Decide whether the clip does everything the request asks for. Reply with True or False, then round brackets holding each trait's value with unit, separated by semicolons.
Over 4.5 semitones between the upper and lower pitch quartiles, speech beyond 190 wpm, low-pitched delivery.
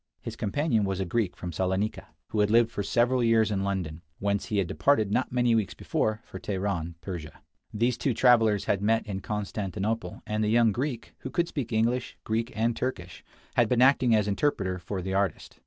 False (3.4 semitones; 200 wpm; 105 Hz)